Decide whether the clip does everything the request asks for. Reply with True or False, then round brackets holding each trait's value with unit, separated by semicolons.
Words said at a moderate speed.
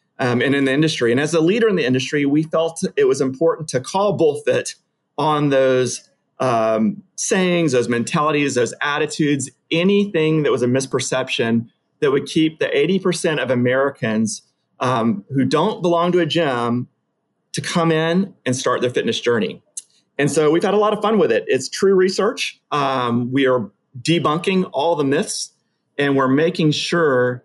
True (175 wpm)